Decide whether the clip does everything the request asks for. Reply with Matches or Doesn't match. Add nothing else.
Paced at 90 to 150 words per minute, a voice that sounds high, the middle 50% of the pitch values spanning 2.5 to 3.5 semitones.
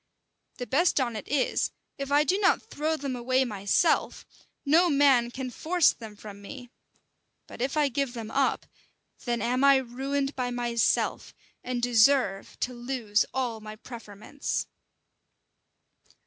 Matches